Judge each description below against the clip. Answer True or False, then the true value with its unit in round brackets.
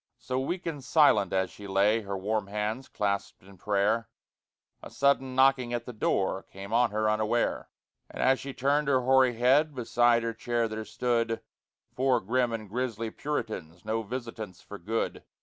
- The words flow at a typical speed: True (170 wpm)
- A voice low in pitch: True (115 Hz)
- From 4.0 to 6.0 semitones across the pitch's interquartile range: False (3.5 semitones)